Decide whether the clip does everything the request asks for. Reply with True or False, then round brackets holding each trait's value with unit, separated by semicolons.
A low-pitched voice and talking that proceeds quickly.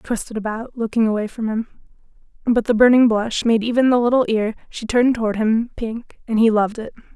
False (225 Hz; 210 wpm)